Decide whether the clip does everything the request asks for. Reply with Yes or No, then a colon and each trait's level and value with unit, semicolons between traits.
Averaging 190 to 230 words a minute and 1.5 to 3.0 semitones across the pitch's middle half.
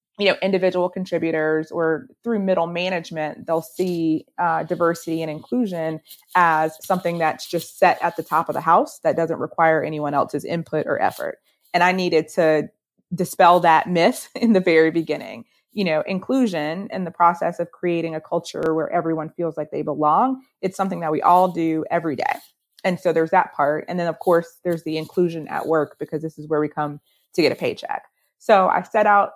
Yes: average, 195 wpm; narrow, 2.6 semitones